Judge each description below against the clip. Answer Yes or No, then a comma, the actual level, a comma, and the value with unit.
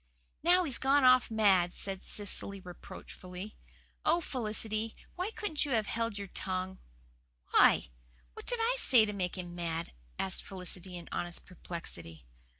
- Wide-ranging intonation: Yes, wide, 5.8 semitones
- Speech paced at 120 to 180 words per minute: Yes, average, 150 wpm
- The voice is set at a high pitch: Yes, high, 200 Hz